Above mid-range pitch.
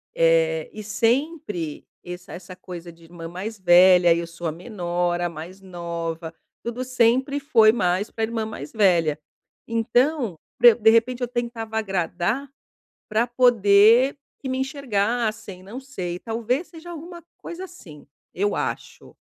Yes: high, 215 Hz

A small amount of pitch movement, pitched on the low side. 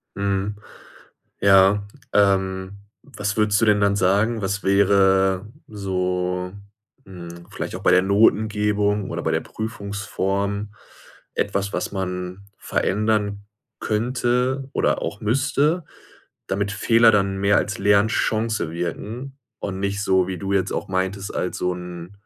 Yes: narrow, 1.8 semitones; low, 100 Hz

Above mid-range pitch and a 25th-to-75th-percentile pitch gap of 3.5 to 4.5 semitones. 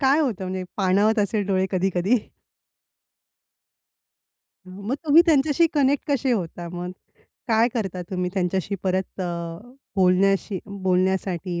Yes: high, 195 Hz; average, 3.8 semitones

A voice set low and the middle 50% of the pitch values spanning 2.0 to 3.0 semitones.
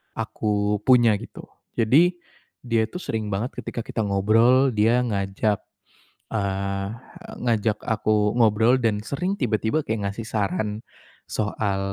Yes: low, 110 Hz; narrow, 2.4 semitones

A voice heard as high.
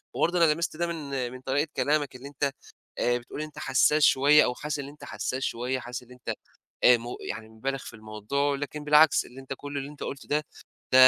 No: medium, 140 Hz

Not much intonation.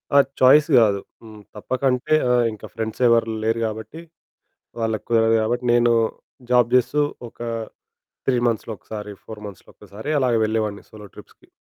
Yes: narrow, 2.2 semitones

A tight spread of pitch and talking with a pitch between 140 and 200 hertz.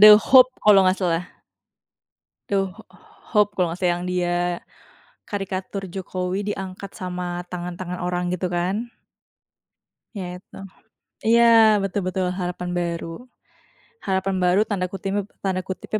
Yes: narrow, 1.7 semitones; medium, 185 Hz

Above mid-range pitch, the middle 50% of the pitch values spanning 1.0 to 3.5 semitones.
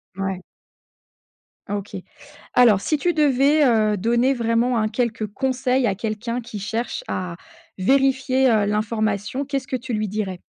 No: high, 230 Hz; average, 3.9 semitones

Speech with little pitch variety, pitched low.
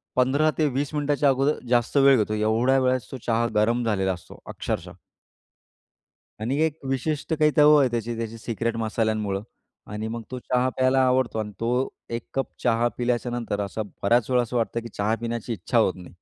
No: average, 3.0 semitones; low, 120 Hz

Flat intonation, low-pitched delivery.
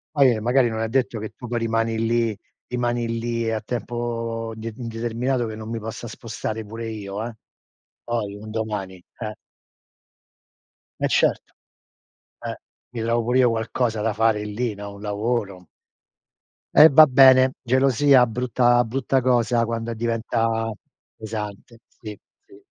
Yes: narrow, 1.7 semitones; low, 115 Hz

